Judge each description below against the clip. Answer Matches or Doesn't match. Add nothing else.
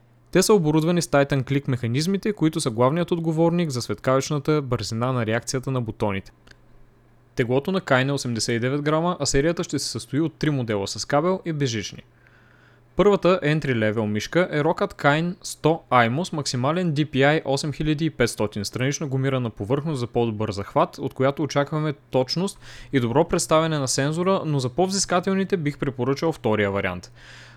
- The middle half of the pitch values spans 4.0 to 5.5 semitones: Matches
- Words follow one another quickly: Doesn't match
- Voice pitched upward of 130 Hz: Matches